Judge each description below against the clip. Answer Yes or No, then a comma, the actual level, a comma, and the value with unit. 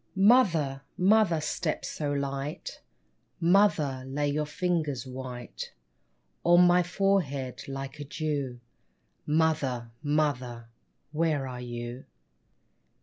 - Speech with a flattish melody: No, average, 4.1 semitones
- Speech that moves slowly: Yes, slow, 95 wpm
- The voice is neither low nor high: Yes, medium, 145 Hz